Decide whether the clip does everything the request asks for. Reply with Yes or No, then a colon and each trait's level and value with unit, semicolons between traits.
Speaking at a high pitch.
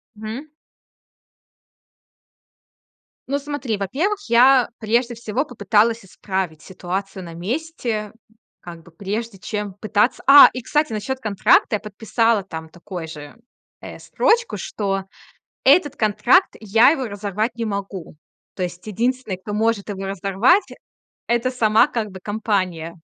Yes: high, 215 Hz